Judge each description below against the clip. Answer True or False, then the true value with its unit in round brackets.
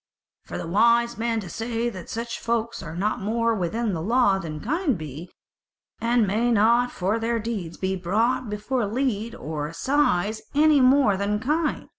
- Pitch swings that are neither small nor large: True (3.6 semitones)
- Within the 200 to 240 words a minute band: False (165 wpm)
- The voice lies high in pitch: True (225 Hz)